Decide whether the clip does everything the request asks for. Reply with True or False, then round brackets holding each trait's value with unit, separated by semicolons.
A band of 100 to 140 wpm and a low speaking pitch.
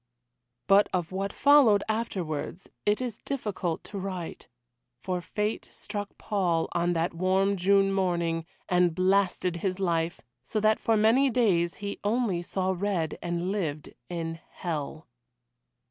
False (135 wpm; 185 Hz)